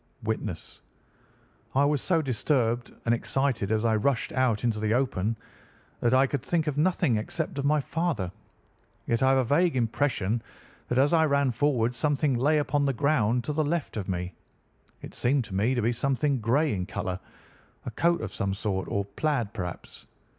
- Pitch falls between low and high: No, low, 130 Hz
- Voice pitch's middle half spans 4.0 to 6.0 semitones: Yes, average, 4.6 semitones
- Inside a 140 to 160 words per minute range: No, average, 190 wpm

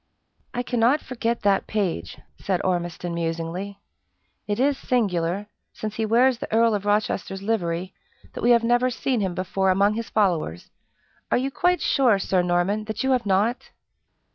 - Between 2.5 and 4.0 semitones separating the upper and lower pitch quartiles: No, average, 4.4 semitones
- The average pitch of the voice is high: Yes, high, 205 Hz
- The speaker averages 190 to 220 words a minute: No, average, 165 wpm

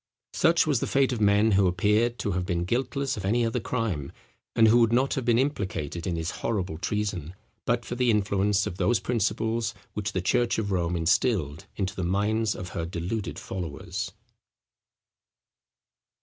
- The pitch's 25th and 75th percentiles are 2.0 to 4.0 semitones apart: No, average, 4.4 semitones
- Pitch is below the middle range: Yes, low, 105 Hz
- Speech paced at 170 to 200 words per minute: Yes, average, 175 wpm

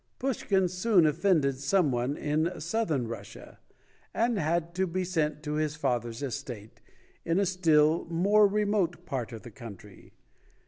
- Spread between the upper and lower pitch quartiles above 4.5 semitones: Yes, average, 5.3 semitones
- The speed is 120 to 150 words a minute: Yes, average, 145 wpm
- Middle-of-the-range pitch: Yes, medium, 160 Hz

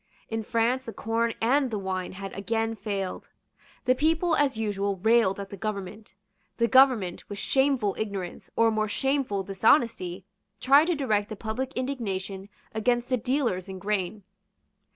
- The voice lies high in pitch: Yes, high, 220 Hz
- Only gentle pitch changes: No, average, 4.3 semitones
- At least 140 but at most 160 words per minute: Yes, average, 150 wpm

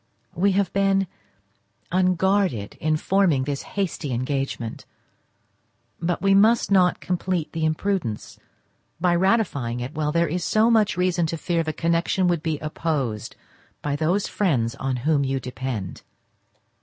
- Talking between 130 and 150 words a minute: Yes, average, 140 wpm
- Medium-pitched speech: Yes, medium, 165 Hz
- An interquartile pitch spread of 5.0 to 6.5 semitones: Yes, wide, 5.5 semitones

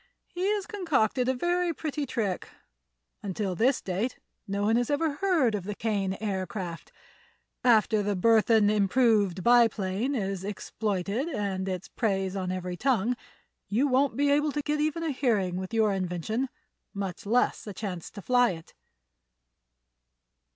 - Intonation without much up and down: No, average, 5.3 semitones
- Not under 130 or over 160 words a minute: Yes, average, 150 wpm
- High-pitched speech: Yes, high, 220 Hz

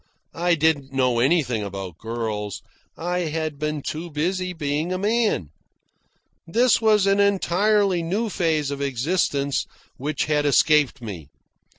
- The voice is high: No, medium, 155 Hz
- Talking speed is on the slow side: Yes, slow, 130 wpm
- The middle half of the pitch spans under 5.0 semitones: No, wide, 5.4 semitones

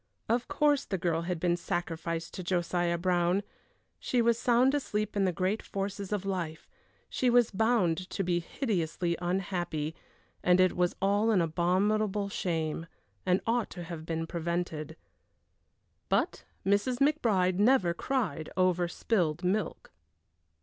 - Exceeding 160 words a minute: No, average, 140 wpm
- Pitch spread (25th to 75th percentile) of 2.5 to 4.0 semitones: Yes, average, 3.6 semitones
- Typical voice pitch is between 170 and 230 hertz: Yes, medium, 185 Hz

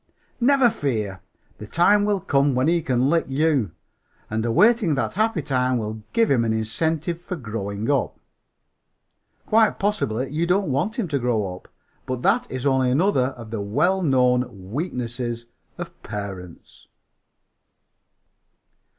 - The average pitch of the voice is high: No, low, 130 Hz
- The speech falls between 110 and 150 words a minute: Yes, average, 140 wpm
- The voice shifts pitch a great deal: Yes, wide, 7.0 semitones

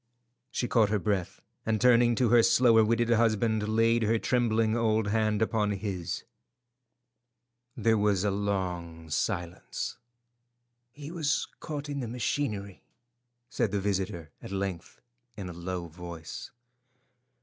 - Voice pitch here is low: Yes, low, 110 Hz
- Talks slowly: Yes, slow, 130 wpm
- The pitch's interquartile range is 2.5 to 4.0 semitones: Yes, average, 3.4 semitones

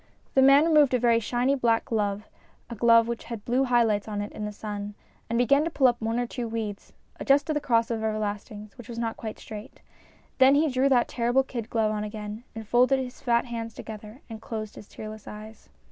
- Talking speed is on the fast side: Yes, fast, 225 wpm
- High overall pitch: Yes, high, 230 Hz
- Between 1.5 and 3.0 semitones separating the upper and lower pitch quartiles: Yes, average, 2.7 semitones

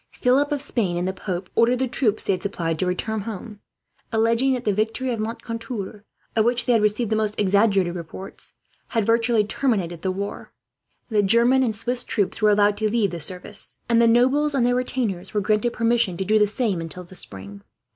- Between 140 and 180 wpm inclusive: No, fast, 205 wpm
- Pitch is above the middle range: Yes, high, 215 Hz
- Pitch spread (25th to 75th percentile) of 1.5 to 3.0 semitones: No, average, 3.6 semitones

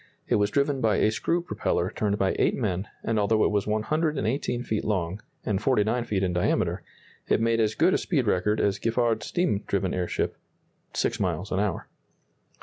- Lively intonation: No, average, 3.3 semitones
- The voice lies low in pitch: Yes, low, 110 Hz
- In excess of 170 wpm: Yes, average, 185 wpm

